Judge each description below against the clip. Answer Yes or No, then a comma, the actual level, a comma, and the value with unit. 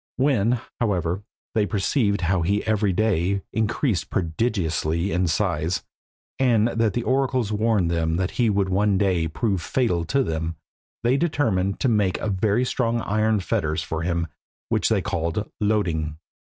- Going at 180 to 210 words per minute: No, average, 150 wpm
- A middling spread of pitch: Yes, average, 4.8 semitones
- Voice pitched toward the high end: No, low, 100 Hz